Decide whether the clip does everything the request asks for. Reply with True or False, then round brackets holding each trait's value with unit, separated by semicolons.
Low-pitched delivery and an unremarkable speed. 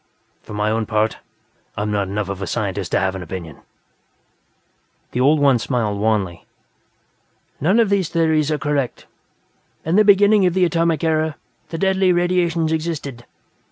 False (150 Hz; 160 wpm)